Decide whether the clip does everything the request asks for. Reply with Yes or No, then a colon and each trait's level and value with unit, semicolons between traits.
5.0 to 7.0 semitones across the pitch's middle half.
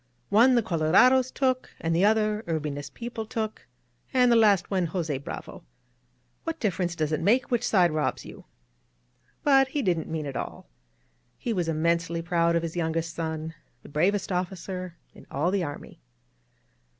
Yes: average, 5.3 semitones